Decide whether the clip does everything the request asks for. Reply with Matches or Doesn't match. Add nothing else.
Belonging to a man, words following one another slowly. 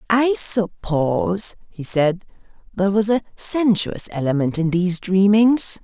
Matches